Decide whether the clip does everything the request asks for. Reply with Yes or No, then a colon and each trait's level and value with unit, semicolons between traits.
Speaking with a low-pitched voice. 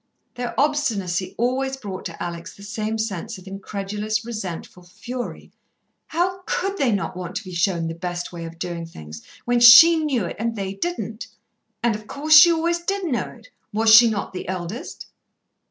No: high, 215 Hz